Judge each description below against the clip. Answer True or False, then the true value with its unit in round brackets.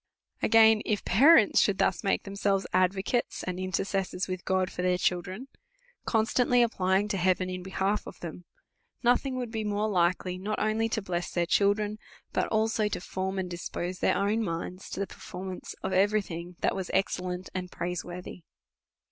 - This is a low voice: False (190 Hz)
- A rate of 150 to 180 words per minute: True (175 wpm)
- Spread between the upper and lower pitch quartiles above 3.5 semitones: False (2.7 semitones)